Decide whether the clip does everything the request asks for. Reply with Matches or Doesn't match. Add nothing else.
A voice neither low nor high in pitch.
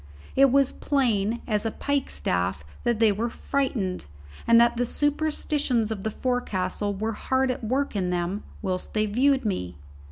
Doesn't match